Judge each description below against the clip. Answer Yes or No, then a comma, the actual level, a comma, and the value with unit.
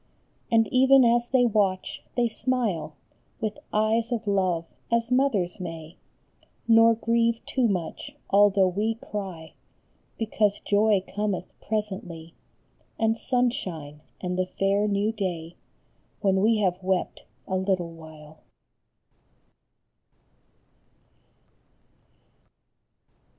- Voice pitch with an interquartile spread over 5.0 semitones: No, average, 3.8 semitones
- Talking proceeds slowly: Yes, slow, 100 wpm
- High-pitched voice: Yes, high, 205 Hz